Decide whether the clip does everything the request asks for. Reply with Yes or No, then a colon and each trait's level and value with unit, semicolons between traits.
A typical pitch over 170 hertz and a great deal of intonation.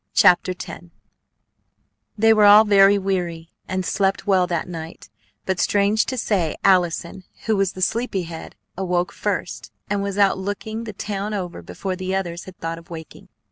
No: high, 190 Hz; narrow, 2.5 semitones